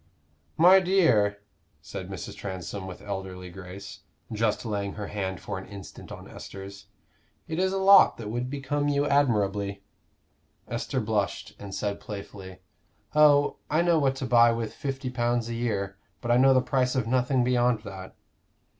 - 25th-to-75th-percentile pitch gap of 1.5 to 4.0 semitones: No, average, 5.1 semitones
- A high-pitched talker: No, low, 115 Hz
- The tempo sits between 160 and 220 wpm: Yes, average, 165 wpm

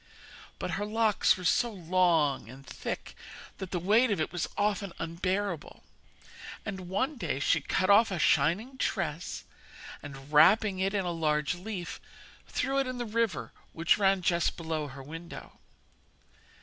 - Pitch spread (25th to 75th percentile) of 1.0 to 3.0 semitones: No, average, 4.3 semitones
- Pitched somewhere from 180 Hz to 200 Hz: Yes, medium, 185 Hz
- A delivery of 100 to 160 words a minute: Yes, average, 155 wpm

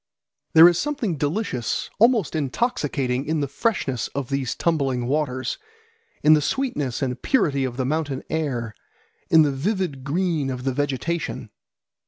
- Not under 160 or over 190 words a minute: No, average, 145 wpm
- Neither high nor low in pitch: Yes, medium, 145 Hz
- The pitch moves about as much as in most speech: Yes, average, 4.2 semitones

